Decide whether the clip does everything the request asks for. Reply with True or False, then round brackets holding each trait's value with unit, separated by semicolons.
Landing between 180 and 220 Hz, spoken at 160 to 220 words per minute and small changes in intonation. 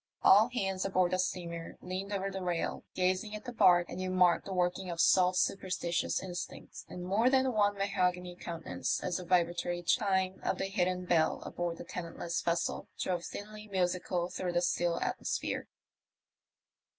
True (185 Hz; 170 wpm; 1.8 semitones)